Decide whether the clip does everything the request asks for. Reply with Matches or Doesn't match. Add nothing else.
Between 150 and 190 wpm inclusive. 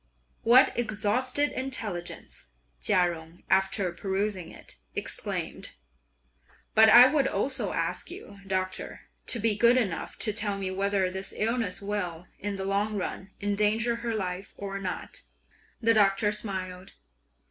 Doesn't match